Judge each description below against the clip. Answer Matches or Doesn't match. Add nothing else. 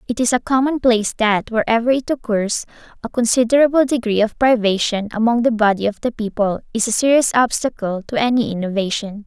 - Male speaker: Doesn't match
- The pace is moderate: Matches